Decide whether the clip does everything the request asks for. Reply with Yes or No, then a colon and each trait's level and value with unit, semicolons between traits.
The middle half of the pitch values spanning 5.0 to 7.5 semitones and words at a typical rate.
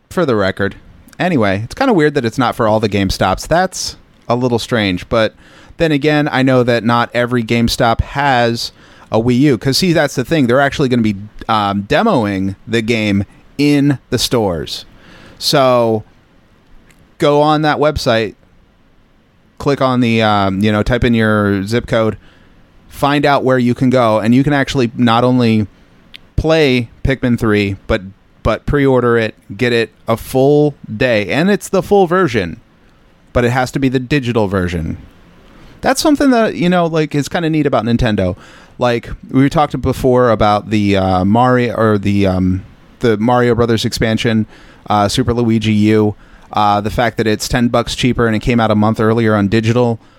No: average, 3.9 semitones; average, 180 wpm